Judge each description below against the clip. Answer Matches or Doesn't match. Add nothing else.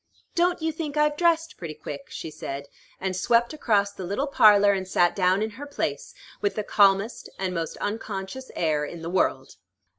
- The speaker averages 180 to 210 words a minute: Matches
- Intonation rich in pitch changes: Matches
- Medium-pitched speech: Doesn't match